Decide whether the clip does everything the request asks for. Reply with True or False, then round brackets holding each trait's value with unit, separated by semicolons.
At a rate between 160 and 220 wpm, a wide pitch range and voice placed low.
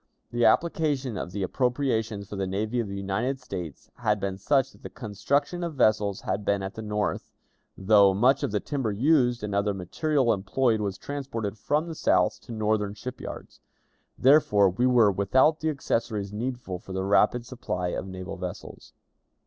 False (180 wpm; 4.7 semitones; 110 Hz)